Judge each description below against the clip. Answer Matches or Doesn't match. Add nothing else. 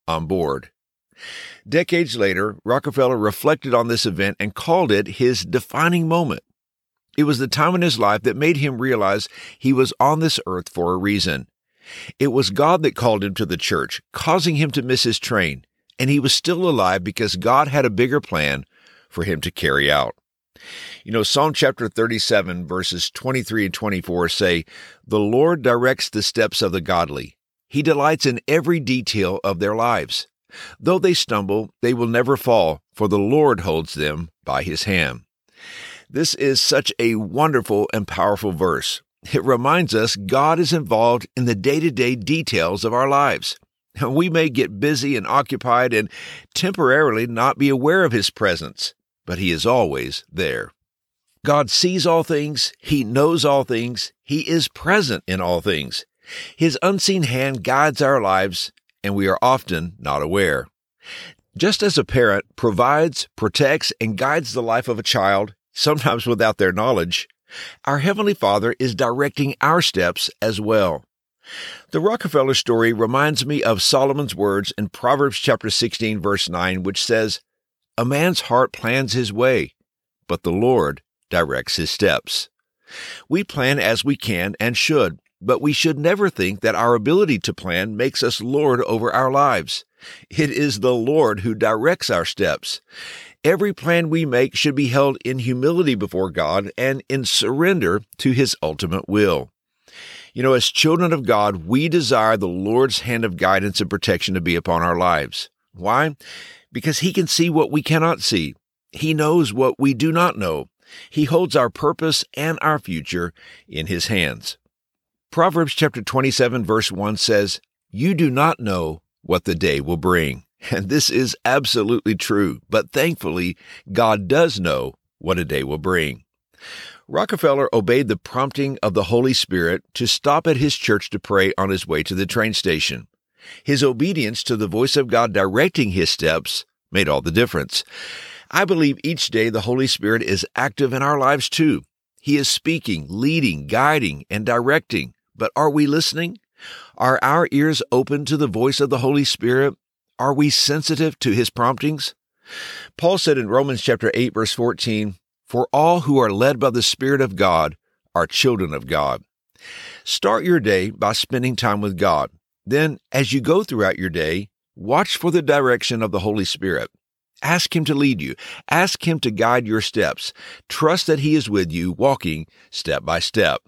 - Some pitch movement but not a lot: Doesn't match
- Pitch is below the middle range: Matches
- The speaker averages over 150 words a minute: Matches